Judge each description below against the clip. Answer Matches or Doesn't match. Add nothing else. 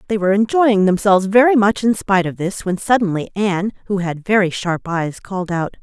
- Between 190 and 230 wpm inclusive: Matches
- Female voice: Matches